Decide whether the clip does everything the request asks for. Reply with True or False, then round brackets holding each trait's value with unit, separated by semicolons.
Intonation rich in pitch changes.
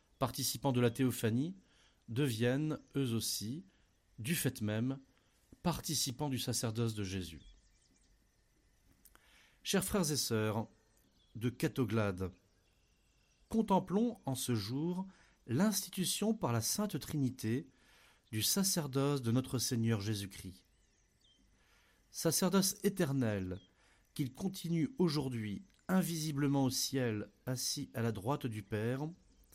True (6.2 semitones)